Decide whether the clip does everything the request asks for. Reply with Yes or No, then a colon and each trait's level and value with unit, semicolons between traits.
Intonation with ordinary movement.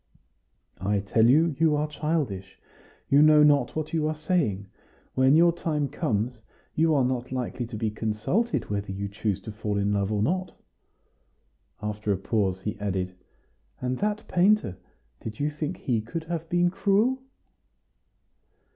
No: wide, 7.3 semitones